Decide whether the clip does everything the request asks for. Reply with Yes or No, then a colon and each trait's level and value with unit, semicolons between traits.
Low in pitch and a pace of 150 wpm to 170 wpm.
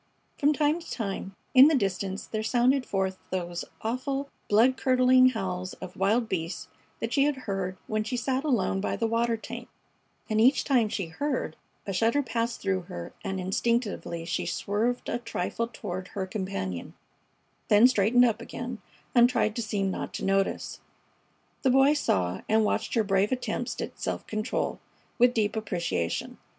No: high, 220 Hz; average, 165 wpm